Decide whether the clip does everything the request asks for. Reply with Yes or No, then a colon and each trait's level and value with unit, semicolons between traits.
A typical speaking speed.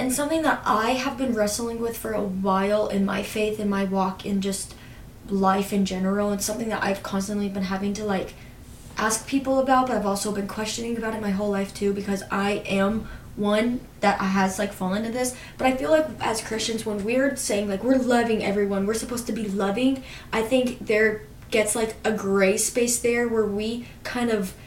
No: fast, 210 wpm